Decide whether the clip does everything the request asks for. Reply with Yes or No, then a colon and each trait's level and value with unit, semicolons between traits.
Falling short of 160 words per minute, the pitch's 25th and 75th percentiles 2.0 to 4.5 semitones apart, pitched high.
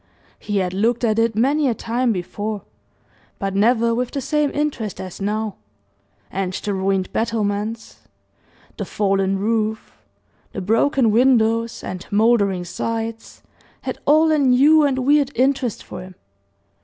Yes: average, 140 wpm; average, 3.9 semitones; high, 225 Hz